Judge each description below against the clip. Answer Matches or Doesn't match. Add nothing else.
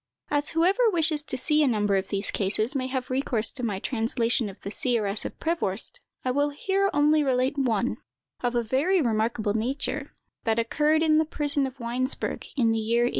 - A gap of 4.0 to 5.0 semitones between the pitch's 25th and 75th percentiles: Matches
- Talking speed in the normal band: Matches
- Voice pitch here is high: Matches